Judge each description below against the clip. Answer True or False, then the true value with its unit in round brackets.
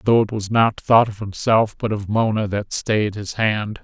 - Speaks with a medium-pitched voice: False (105 Hz)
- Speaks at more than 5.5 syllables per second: False (4.4 syllables/s)